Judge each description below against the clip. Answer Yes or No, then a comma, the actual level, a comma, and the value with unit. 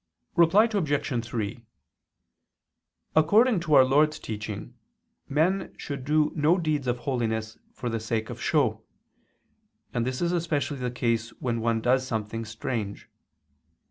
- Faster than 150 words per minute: No, slow, 135 wpm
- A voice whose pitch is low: Yes, low, 130 Hz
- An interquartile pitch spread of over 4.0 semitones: Yes, average, 5.2 semitones